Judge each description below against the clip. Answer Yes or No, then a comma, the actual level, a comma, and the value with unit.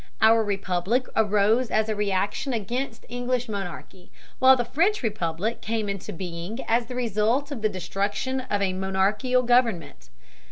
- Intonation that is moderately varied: Yes, average, 4.0 semitones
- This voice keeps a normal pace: Yes, average, 150 wpm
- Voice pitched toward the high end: Yes, high, 215 Hz